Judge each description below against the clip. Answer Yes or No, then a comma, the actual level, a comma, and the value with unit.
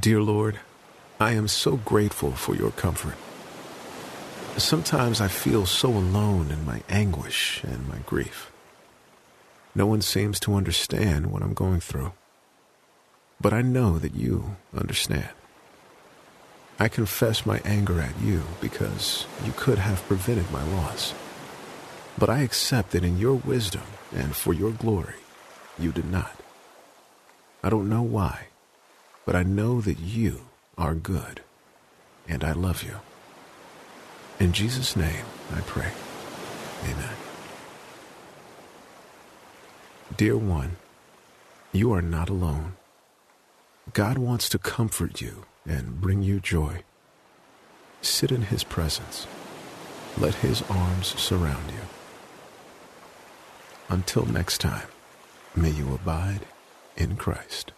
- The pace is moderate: No, slow, 120 wpm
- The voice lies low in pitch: Yes, low, 100 Hz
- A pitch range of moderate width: Yes, average, 4.1 semitones